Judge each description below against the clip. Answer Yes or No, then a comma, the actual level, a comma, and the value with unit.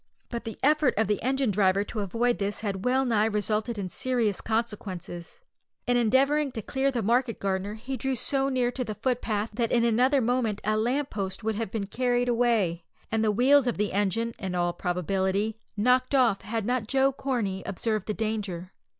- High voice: Yes, high, 225 Hz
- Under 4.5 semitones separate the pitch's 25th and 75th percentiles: Yes, average, 3.6 semitones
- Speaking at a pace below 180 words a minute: No, average, 195 wpm